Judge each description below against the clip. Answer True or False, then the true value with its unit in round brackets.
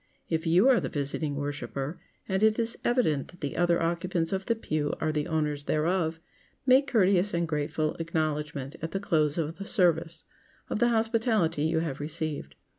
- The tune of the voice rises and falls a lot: False (4.2 semitones)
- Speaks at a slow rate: False (180 wpm)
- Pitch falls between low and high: True (165 Hz)